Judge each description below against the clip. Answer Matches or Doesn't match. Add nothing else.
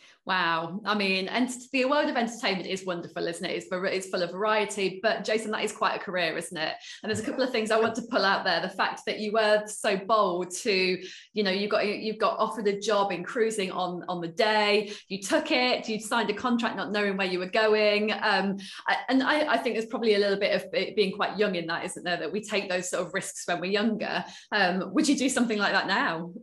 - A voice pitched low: Doesn't match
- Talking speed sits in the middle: Doesn't match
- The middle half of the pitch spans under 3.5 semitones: Matches